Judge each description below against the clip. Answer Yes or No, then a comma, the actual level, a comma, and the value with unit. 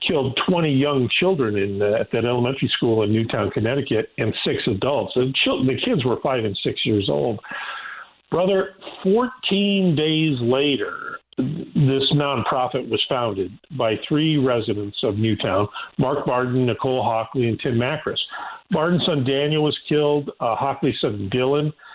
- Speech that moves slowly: No, average, 150 wpm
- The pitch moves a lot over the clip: No, average, 4.7 semitones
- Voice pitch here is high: No, low, 135 Hz